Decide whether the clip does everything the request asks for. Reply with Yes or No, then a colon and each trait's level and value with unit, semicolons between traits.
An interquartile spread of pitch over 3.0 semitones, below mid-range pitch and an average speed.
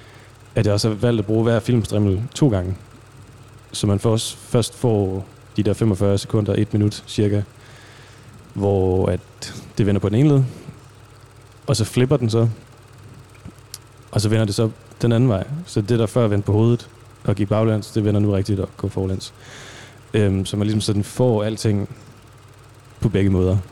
No: narrow, 2.4 semitones; low, 110 Hz; average, 180 wpm